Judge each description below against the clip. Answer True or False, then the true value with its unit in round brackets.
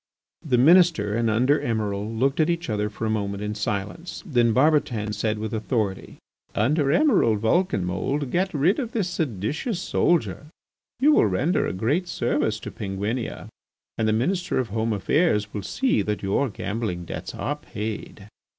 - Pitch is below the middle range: True (115 Hz)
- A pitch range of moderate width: False (6.9 semitones)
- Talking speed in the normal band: True (165 wpm)